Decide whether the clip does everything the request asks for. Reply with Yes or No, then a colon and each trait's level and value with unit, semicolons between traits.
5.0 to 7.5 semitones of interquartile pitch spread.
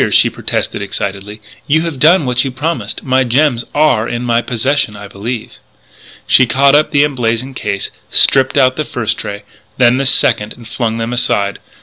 No: average, 3.5 semitones